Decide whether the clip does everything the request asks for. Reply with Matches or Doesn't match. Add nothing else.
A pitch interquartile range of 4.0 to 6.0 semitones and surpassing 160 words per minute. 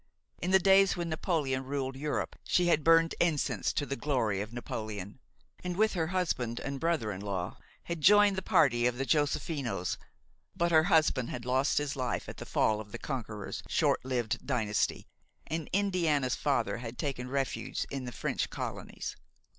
Matches